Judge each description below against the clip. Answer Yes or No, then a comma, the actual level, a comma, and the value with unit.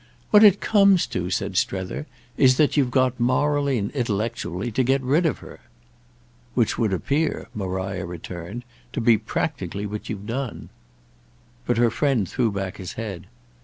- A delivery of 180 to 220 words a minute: No, average, 160 wpm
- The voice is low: Yes, low, 115 Hz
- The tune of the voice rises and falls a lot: Yes, wide, 5.8 semitones